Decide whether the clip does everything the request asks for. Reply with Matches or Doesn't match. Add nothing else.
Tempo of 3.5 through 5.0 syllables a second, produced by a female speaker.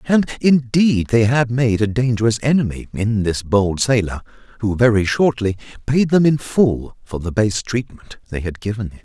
Doesn't match